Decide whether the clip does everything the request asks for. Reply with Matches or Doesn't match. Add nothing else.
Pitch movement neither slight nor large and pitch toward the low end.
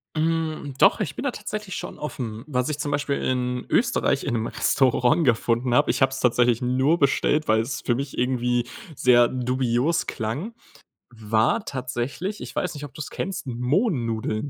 Matches